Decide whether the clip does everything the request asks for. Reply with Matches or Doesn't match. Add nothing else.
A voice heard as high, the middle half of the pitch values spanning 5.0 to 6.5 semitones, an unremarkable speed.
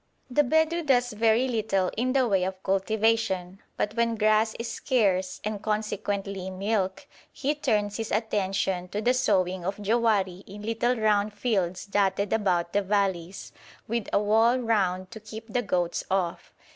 Doesn't match